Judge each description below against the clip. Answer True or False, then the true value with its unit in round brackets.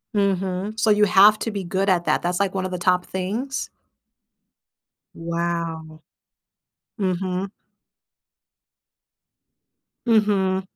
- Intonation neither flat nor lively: False (2.3 semitones)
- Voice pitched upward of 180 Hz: True (190 Hz)